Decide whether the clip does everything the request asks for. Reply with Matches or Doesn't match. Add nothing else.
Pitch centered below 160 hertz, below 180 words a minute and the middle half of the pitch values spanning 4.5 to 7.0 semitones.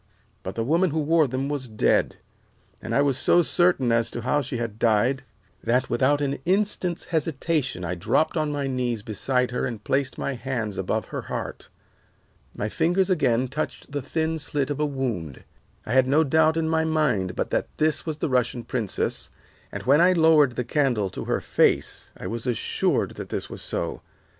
Doesn't match